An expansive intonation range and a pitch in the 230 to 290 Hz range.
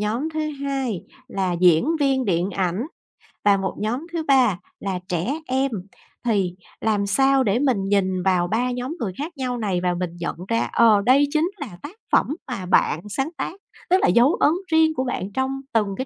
Yes: wide, 6.0 semitones; high, 235 Hz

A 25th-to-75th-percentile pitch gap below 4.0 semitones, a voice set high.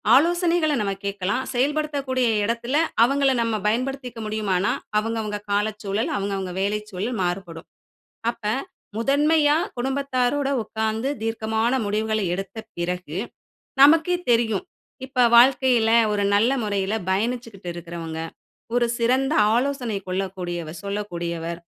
No: average, 4.8 semitones; high, 220 Hz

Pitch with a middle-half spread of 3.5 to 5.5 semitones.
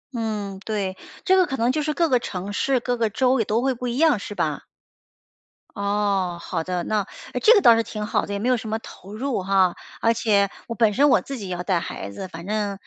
Yes: average, 4.1 semitones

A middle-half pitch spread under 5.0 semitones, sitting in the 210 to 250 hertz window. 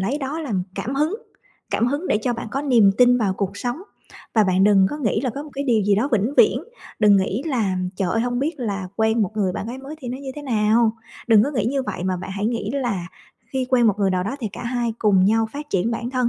Yes: average, 4.5 semitones; high, 230 Hz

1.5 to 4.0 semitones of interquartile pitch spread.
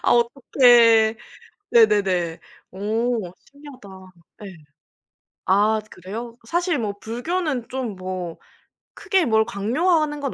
No: average, 5.3 semitones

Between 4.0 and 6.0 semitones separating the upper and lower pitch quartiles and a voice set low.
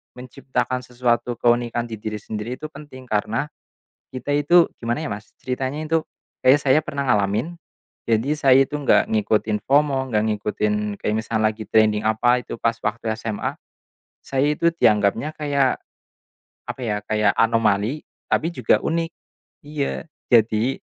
Yes: average, 4.4 semitones; low, 120 Hz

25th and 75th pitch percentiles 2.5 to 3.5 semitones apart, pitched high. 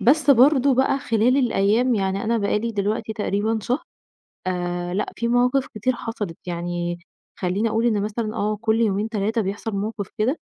Yes: average, 3.1 semitones; high, 220 Hz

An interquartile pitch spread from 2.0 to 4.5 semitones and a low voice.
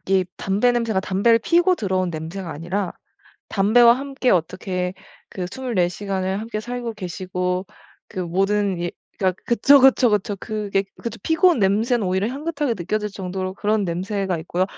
No: average, 4.0 semitones; high, 200 Hz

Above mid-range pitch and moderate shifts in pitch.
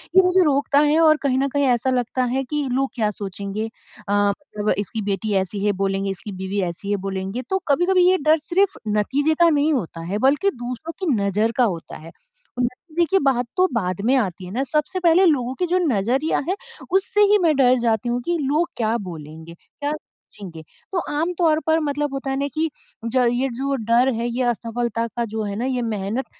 No: very high, 250 Hz; wide, 6.6 semitones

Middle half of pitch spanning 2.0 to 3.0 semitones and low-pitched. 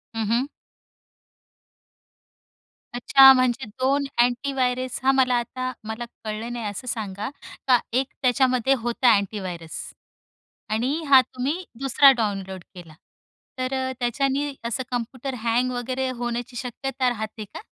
No: average, 2.7 semitones; high, 245 Hz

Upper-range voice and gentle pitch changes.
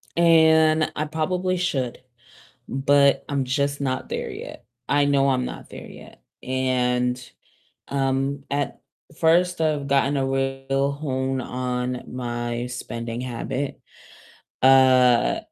No: low, 135 Hz; narrow, 2.1 semitones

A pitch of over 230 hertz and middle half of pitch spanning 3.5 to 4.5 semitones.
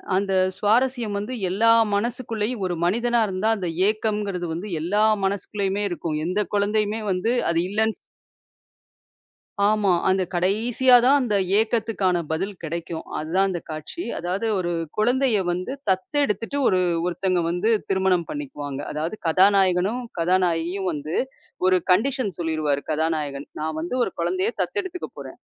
No: high, 195 Hz; average, 4.1 semitones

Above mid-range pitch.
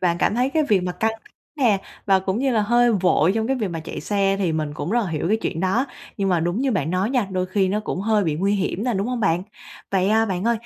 Yes: high, 195 Hz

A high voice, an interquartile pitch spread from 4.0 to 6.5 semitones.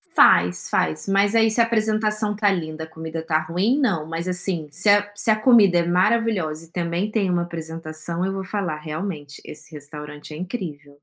No: medium, 175 Hz; average, 4.6 semitones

